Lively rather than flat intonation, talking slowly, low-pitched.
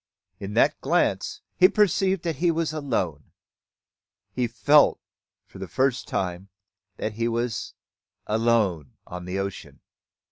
Yes: wide, 7.8 semitones; slow, 130 wpm; low, 115 Hz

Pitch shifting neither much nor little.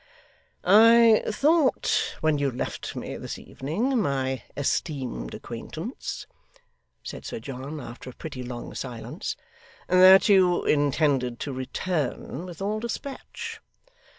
No: wide, 8.1 semitones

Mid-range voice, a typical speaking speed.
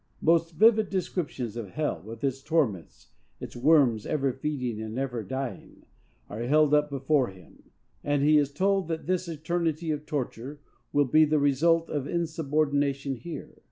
Yes: medium, 145 Hz; average, 160 wpm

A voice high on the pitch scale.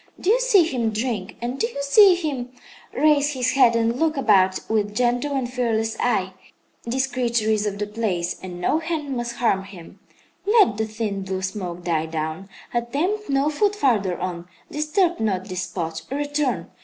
Yes: high, 235 Hz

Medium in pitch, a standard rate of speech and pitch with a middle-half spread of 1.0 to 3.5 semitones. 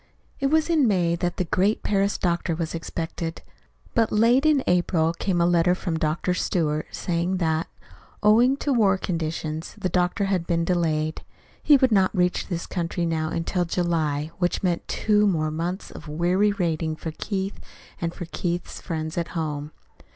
Yes: medium, 175 Hz; average, 170 wpm; average, 3.0 semitones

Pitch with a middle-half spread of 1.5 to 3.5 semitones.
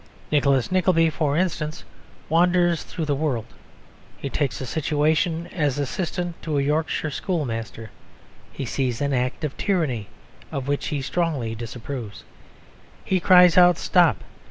No: average, 4.2 semitones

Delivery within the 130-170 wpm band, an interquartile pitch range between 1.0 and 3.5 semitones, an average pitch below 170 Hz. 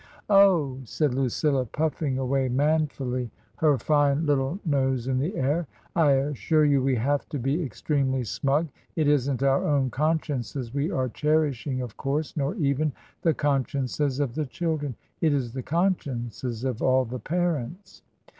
Yes: average, 155 wpm; average, 2.8 semitones; medium, 140 Hz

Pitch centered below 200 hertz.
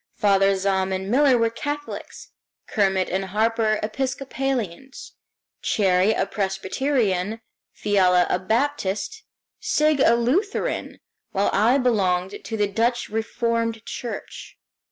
No: high, 220 Hz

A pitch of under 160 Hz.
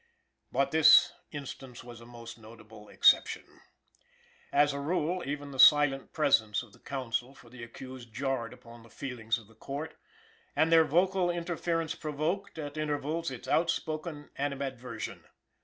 Yes: medium, 140 Hz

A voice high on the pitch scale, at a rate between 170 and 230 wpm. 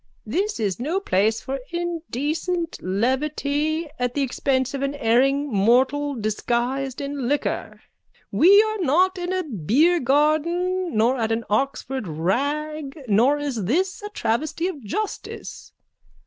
No: very high, 280 Hz; slow, 135 wpm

